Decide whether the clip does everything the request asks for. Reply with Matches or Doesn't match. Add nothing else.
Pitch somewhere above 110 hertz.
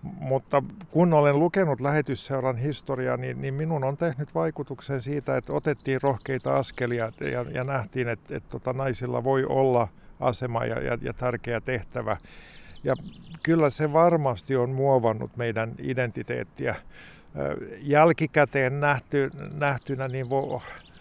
Matches